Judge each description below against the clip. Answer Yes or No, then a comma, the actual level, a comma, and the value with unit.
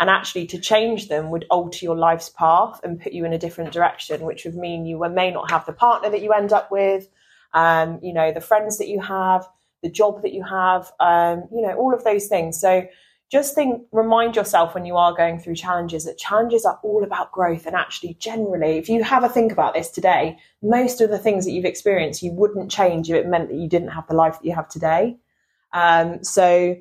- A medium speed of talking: No, fast, 235 wpm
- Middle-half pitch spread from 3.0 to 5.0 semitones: Yes, average, 3.9 semitones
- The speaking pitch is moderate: Yes, medium, 180 Hz